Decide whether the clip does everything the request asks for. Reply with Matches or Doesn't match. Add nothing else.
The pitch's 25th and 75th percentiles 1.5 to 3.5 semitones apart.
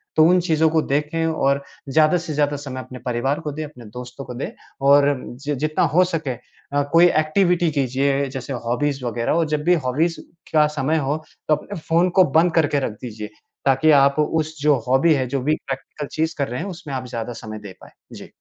Matches